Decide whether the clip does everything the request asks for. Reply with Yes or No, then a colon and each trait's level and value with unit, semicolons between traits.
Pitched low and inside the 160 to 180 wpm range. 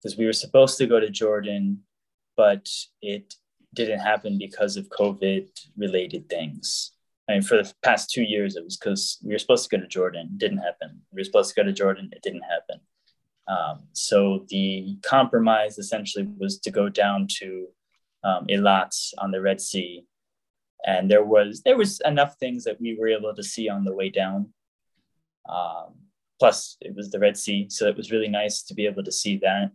No: low, 105 Hz; average, 200 wpm